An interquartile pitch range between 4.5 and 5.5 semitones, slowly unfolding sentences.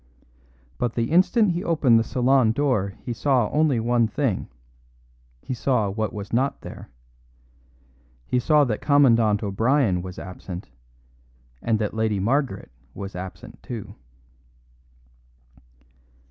Yes: average, 5.0 semitones; slow, 120 wpm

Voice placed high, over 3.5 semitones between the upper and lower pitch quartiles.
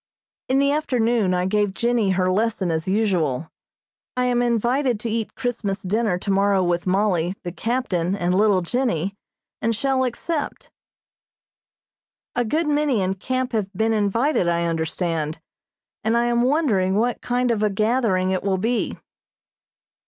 Yes: high, 215 Hz; average, 4.7 semitones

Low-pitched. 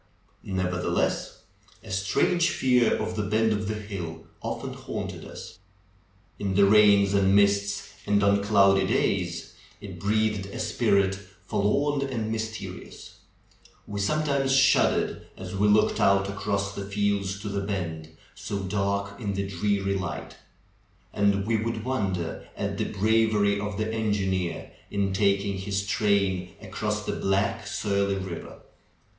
Yes: low, 100 Hz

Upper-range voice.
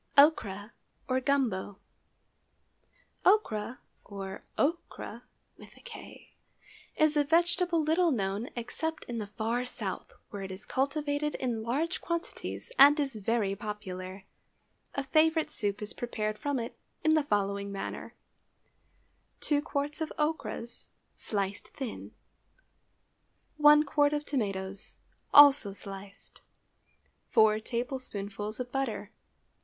Yes: high, 245 Hz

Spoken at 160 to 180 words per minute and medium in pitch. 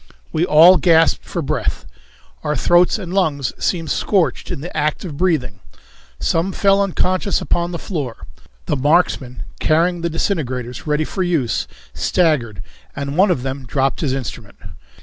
No: average, 150 wpm; medium, 160 Hz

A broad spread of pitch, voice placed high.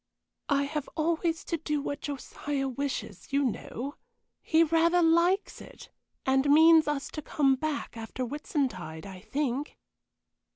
No: average, 3.2 semitones; very high, 285 Hz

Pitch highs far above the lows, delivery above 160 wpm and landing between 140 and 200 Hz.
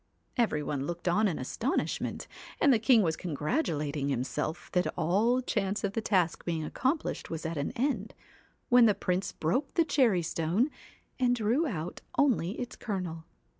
Yes: wide, 7.0 semitones; average, 170 wpm; high, 190 Hz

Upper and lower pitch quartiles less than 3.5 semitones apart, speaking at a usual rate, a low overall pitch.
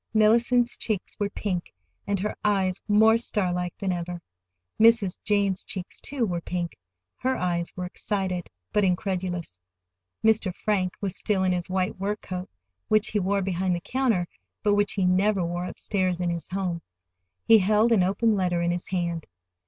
No: average, 2.8 semitones; average, 170 wpm; high, 190 Hz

